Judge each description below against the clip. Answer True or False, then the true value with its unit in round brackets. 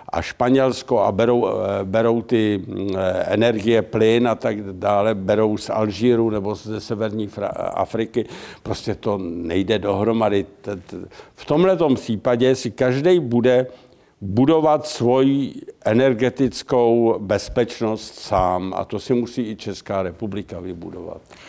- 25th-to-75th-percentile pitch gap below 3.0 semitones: False (3.5 semitones)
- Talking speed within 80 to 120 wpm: True (115 wpm)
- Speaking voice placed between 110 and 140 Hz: True (115 Hz)